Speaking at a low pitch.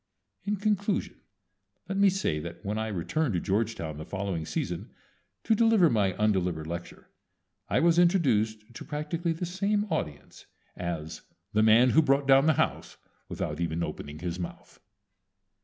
Yes: low, 110 Hz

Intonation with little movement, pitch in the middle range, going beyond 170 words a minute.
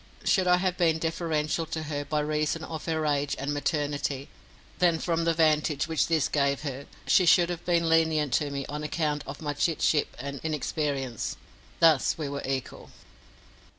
Yes: narrow, 2.1 semitones; medium, 155 Hz; average, 180 wpm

